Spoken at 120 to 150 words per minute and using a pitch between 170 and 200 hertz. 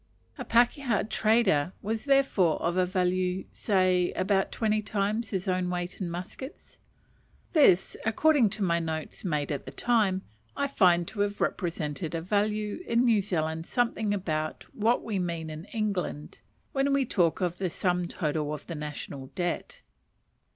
No: average, 160 wpm; medium, 185 Hz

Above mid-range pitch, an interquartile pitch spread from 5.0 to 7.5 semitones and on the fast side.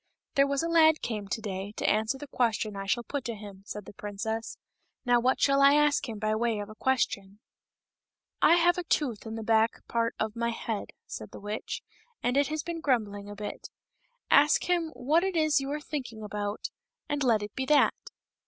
Yes: high, 235 Hz; wide, 5.4 semitones; fast, 225 wpm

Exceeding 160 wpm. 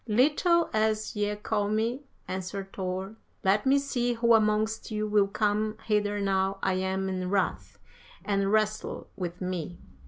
No: average, 150 wpm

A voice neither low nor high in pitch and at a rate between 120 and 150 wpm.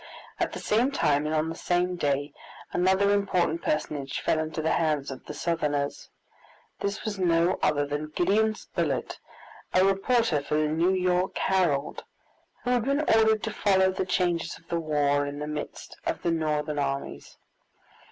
No: medium, 165 Hz; average, 170 wpm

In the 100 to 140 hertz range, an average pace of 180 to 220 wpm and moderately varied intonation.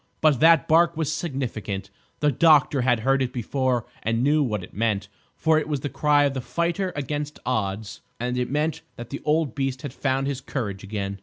Yes: low, 135 Hz; fast, 205 wpm; average, 4.3 semitones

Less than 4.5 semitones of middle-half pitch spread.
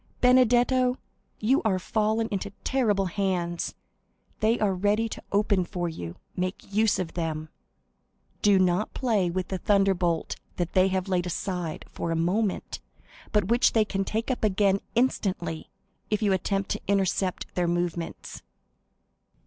Yes: average, 3.3 semitones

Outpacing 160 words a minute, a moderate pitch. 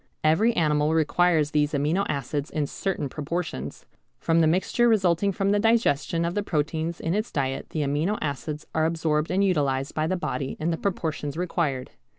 Yes: average, 175 wpm; medium, 160 Hz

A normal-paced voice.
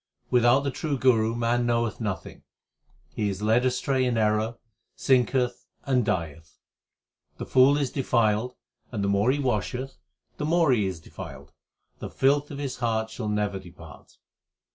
Yes: average, 155 wpm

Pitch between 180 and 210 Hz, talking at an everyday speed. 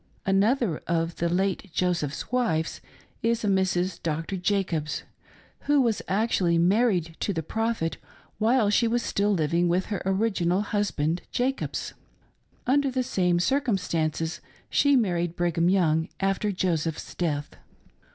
No: high, 190 Hz; slow, 130 wpm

